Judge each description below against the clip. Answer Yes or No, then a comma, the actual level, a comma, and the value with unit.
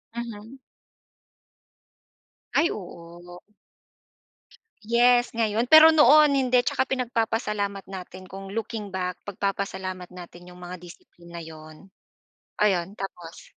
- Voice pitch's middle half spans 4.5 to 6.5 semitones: Yes, average, 4.8 semitones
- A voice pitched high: Yes, high, 200 Hz